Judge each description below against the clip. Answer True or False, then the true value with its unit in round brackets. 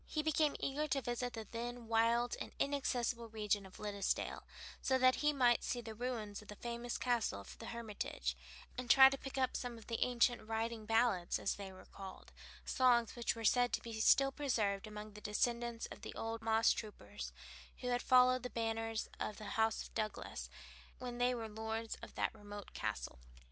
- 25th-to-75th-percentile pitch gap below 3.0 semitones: True (2.5 semitones)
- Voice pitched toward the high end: True (230 Hz)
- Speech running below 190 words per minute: False (195 wpm)